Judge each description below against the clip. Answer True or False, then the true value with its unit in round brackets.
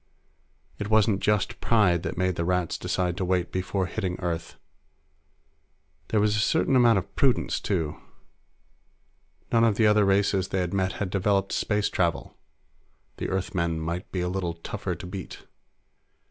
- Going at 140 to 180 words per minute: True (160 wpm)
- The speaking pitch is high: False (95 Hz)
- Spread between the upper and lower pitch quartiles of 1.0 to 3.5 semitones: True (2.8 semitones)